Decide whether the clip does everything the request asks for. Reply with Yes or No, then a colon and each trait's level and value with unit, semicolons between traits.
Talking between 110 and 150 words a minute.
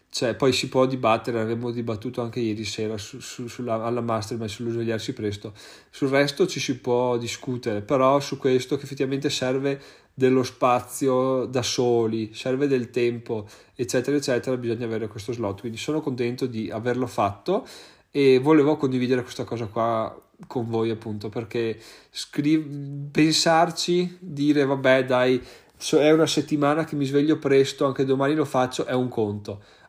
No: average, 160 wpm